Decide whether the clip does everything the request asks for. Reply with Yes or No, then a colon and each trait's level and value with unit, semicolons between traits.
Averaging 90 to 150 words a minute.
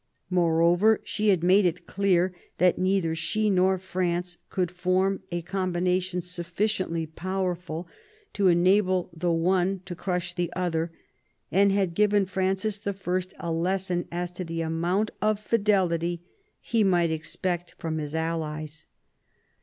Yes: average, 140 wpm